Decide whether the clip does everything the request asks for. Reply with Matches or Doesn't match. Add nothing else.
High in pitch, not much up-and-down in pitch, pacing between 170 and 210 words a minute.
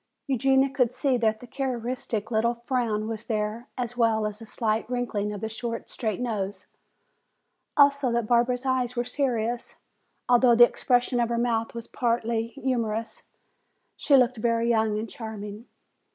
Doesn't match